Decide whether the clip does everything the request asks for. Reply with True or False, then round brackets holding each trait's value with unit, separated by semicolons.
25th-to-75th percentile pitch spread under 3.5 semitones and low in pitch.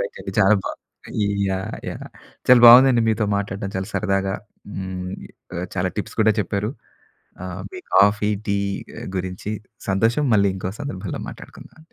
True (2.9 semitones; 100 Hz)